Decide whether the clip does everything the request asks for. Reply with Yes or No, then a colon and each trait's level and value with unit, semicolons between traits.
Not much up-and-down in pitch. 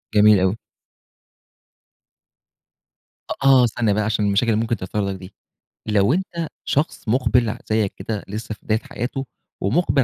No: average, 3.2 semitones